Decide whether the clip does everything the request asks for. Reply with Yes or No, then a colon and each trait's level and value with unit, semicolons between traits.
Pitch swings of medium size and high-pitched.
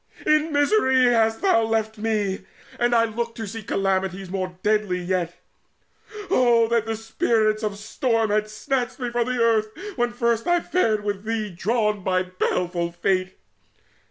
Yes: average, 3.2 semitones; high, 220 Hz